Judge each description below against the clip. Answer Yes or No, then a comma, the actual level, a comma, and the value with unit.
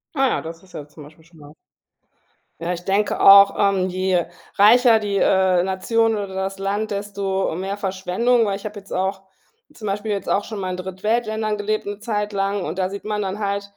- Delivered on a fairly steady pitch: Yes, narrow, 2.0 semitones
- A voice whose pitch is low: No, high, 200 Hz